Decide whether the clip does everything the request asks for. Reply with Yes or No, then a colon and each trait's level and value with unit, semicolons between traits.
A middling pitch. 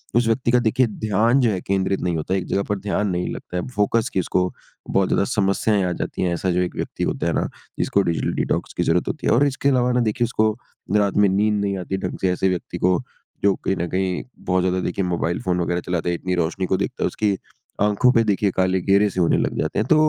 No: very low, 95 Hz